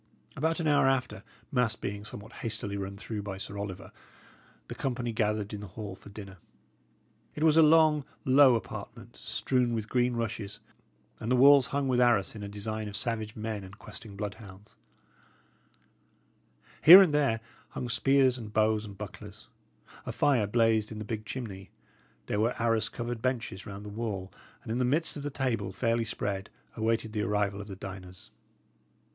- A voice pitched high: No, low, 110 Hz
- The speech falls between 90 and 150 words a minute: No, average, 175 wpm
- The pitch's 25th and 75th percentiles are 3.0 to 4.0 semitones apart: Yes, average, 3.5 semitones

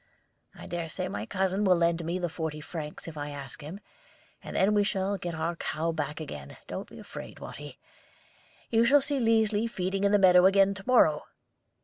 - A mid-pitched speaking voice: Yes, medium, 180 Hz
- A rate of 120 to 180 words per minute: No, average, 200 wpm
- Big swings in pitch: No, average, 3.9 semitones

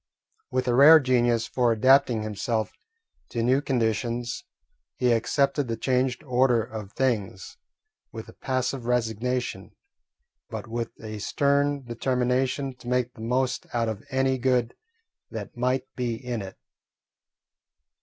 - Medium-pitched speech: No, low, 125 Hz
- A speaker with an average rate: No, slow, 130 wpm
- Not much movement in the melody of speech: Yes, narrow, 2.2 semitones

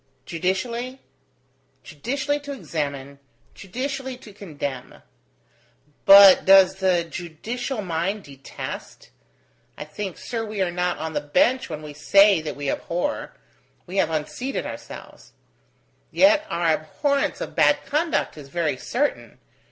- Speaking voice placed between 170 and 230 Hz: Yes, high, 190 Hz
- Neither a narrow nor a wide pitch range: No, wide, 7.9 semitones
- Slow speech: Yes, slow, 125 wpm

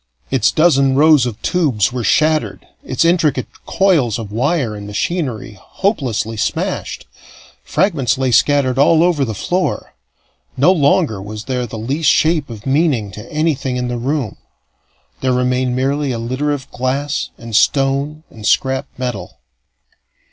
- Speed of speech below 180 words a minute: Yes, average, 145 wpm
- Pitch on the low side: Yes, low, 130 Hz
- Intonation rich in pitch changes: No, average, 4.4 semitones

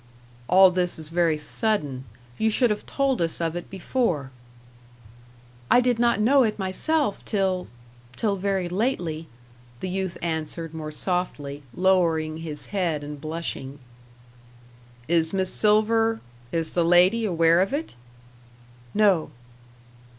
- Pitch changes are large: No, average, 4.7 semitones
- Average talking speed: No, slow, 130 wpm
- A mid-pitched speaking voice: Yes, medium, 180 Hz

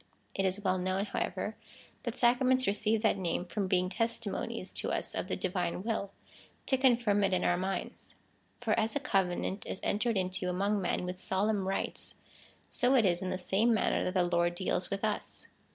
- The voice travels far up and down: No, average, 3.2 semitones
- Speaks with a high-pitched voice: Yes, high, 195 Hz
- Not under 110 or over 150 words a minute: No, average, 190 wpm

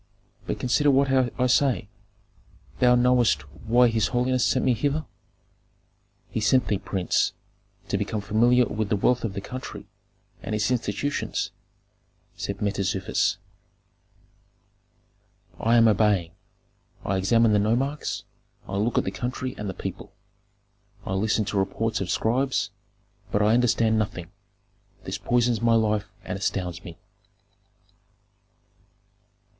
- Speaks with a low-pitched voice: Yes, low, 110 Hz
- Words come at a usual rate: No, slow, 130 wpm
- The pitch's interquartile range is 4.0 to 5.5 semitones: No, average, 3.6 semitones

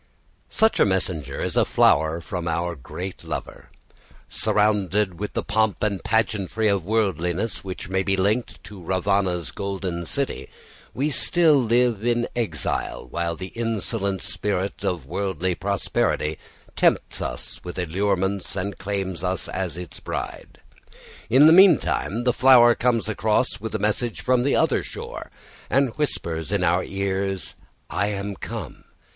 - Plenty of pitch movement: No, average, 3.7 semitones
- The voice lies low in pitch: Yes, low, 100 Hz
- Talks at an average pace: Yes, average, 145 wpm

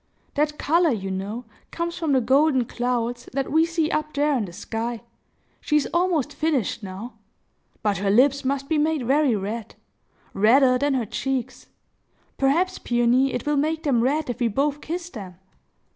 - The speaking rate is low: No, average, 170 wpm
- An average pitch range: Yes, average, 4.4 semitones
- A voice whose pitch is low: No, very high, 270 Hz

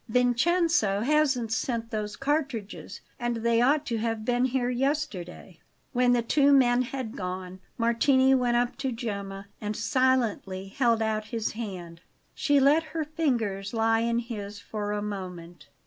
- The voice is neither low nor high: No, high, 235 Hz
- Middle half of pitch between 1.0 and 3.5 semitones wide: No, average, 3.9 semitones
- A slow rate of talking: No, average, 150 wpm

